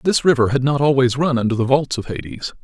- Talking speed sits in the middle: No, fast, 250 wpm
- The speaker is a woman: No, male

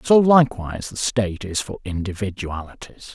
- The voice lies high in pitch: No, low, 105 Hz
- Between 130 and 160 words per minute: Yes, slow, 135 wpm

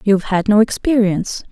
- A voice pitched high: Yes, high, 210 Hz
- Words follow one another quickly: No, average, 160 wpm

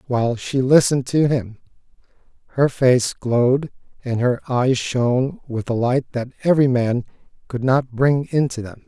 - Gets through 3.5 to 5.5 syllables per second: Yes, 4.6 syllables/s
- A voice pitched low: Yes, low, 125 Hz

